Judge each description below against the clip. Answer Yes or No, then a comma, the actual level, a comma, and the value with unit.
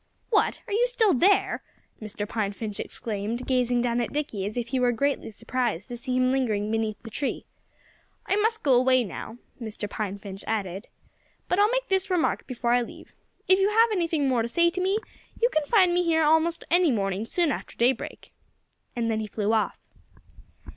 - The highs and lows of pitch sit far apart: Yes, wide, 7.7 semitones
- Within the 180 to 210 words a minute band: Yes, average, 195 wpm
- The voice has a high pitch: Yes, very high, 250 Hz